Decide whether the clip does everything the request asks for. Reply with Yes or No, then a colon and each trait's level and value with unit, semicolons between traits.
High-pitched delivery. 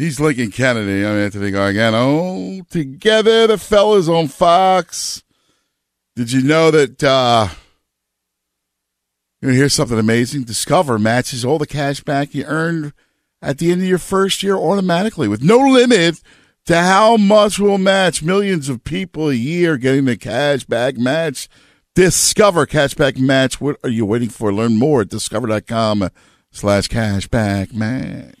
No: medium, 140 Hz